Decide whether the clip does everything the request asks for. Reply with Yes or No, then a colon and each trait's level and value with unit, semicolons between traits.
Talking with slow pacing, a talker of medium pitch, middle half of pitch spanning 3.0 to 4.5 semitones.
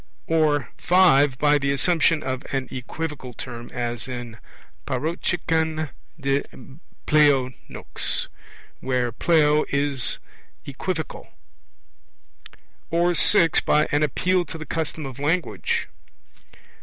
Yes: slow, 105 wpm; medium, 150 Hz; average, 3.6 semitones